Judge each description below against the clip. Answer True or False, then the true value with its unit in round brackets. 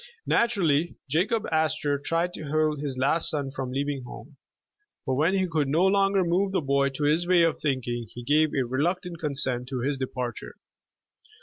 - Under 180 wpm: False (185 wpm)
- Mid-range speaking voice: True (150 Hz)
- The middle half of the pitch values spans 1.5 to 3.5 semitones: False (4.2 semitones)